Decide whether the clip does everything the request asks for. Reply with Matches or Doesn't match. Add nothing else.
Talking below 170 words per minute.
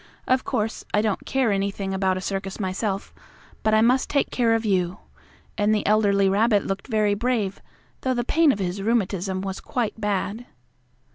Doesn't match